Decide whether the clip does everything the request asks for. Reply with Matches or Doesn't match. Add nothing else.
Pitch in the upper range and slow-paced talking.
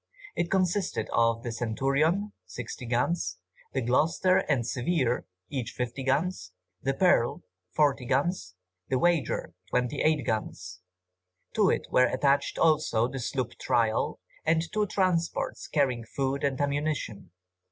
Doesn't match